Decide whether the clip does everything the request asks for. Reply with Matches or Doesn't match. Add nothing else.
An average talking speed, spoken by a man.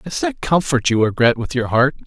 Doesn't match